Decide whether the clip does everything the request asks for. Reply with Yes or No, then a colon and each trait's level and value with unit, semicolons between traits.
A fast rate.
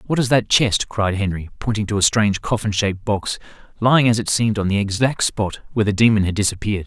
Yes: fast, 225 wpm